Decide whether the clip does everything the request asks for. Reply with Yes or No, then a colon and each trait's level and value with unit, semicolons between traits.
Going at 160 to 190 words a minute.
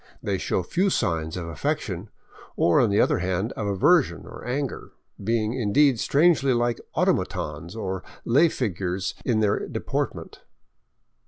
No: average, 140 wpm